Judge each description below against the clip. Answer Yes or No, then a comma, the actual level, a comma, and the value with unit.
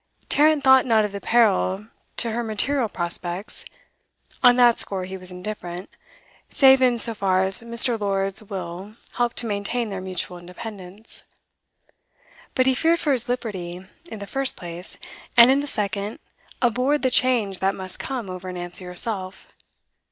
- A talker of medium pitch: No, high, 210 Hz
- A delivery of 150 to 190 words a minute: Yes, average, 160 wpm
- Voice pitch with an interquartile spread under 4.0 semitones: No, average, 4.7 semitones